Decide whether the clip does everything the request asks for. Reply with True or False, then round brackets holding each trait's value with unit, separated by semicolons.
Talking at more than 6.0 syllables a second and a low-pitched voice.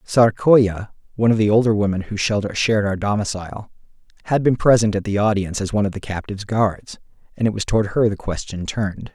True (6.2 syllables/s; 105 Hz)